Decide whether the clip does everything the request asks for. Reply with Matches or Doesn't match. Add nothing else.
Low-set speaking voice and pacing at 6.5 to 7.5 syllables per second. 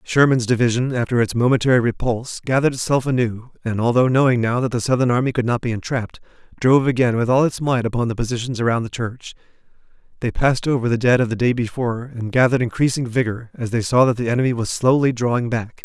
Matches